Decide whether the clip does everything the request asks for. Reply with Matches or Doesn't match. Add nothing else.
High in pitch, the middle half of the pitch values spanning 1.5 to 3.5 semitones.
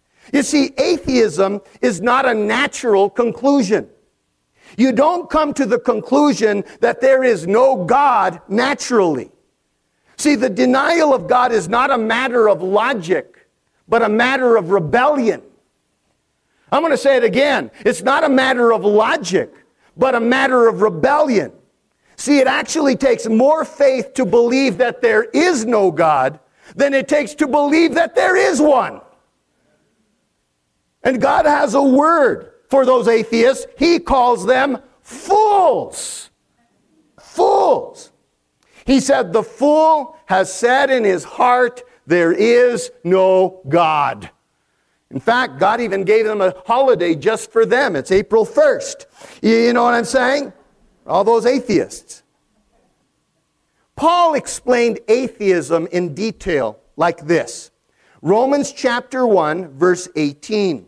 Doesn't match